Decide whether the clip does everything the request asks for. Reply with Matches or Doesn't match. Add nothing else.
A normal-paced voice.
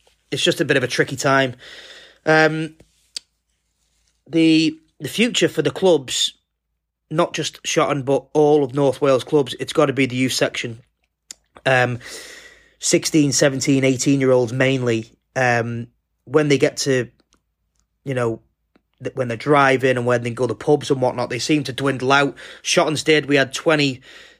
Matches